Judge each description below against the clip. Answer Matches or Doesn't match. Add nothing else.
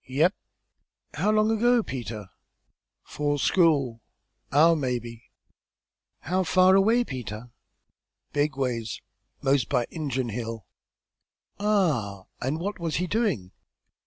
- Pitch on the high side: Doesn't match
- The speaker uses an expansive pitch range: Matches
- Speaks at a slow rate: Matches